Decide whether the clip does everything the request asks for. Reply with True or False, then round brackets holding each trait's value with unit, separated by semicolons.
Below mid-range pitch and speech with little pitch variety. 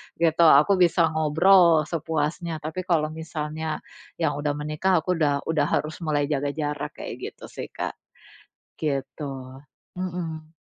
False (155 Hz; 2.1 semitones)